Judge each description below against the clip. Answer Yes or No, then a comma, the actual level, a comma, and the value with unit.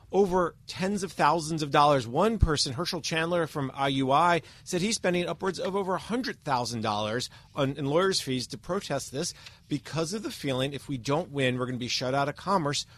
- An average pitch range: Yes, average, 4.7 semitones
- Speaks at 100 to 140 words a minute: No, fast, 205 wpm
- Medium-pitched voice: Yes, medium, 145 Hz